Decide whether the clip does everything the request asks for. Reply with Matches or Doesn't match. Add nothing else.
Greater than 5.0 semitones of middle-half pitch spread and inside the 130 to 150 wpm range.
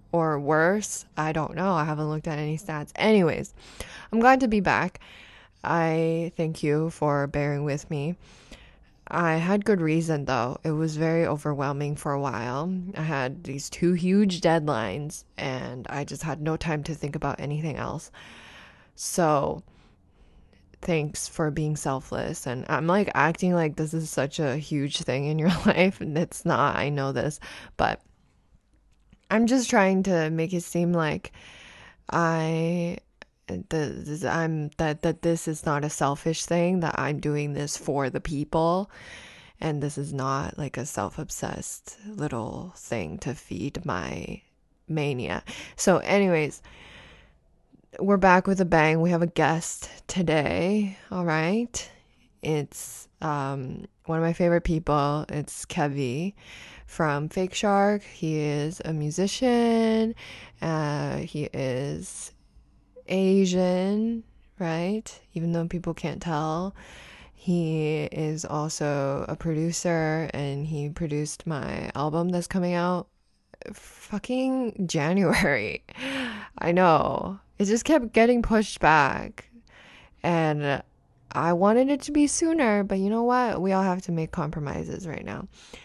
Doesn't match